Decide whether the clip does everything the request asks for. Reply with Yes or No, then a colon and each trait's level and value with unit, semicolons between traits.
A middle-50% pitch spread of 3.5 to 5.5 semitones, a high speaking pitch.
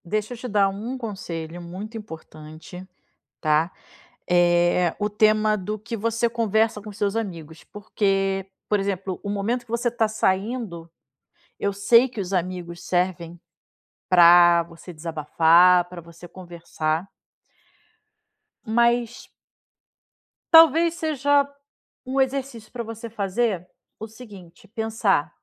Yes: average, 4.6 semitones; high, 200 Hz